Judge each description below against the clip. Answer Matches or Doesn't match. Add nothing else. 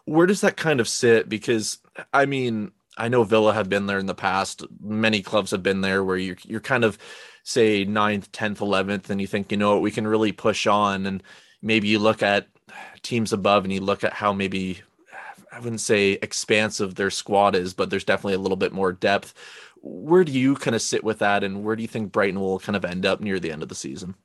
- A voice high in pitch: Doesn't match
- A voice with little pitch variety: Matches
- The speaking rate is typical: Doesn't match